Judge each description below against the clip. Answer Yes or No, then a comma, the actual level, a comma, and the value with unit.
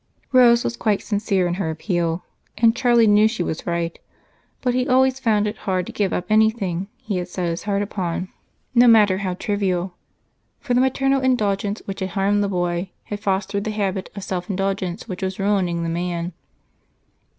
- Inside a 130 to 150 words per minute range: No, average, 185 wpm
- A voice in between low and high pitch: No, high, 200 Hz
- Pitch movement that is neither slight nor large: Yes, average, 3.4 semitones